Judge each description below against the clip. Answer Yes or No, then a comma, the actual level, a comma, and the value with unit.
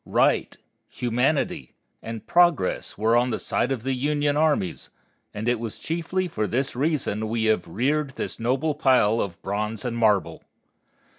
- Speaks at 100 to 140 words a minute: No, average, 155 wpm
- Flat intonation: No, average, 5.1 semitones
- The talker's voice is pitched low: Yes, low, 125 Hz